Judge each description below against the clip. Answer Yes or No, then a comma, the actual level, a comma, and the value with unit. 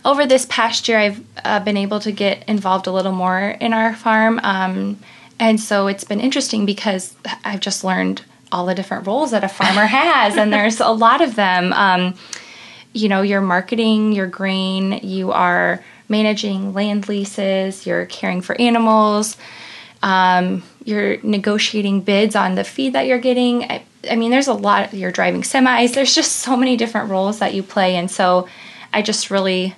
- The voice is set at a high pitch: Yes, high, 205 Hz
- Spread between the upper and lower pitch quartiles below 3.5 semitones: Yes, average, 2.9 semitones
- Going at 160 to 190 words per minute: Yes, average, 185 wpm